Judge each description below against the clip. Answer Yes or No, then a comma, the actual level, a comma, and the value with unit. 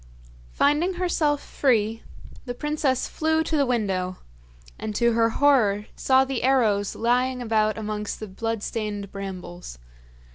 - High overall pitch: Yes, high, 230 Hz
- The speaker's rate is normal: No, slow, 130 wpm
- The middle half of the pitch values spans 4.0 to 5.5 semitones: Yes, average, 4.4 semitones